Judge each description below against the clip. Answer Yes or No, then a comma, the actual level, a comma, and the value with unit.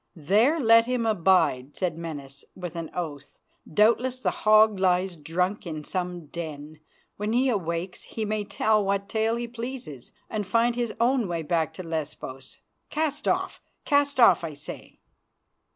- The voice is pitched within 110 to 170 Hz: No, high, 190 Hz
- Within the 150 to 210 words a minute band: Yes, average, 155 wpm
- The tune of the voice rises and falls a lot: Yes, wide, 5.9 semitones